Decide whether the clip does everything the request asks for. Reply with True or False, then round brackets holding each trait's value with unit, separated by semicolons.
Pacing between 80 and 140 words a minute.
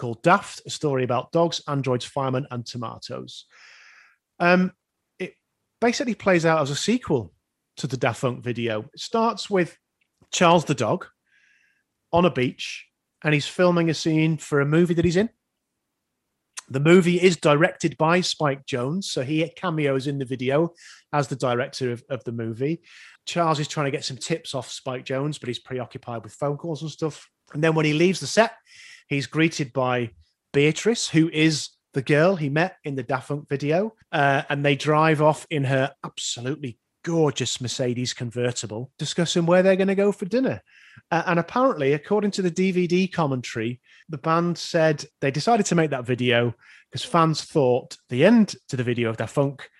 False (180 wpm)